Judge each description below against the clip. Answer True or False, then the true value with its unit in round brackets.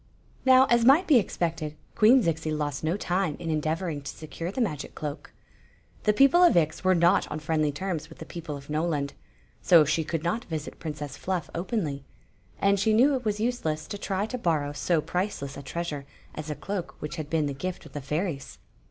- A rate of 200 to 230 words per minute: True (205 wpm)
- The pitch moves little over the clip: False (4.8 semitones)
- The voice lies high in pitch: False (165 Hz)